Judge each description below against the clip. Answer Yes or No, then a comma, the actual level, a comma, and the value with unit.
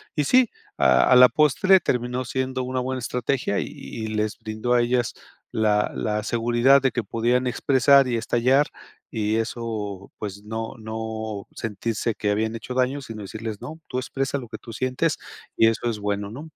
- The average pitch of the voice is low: Yes, low, 120 Hz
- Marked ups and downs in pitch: No, average, 2.9 semitones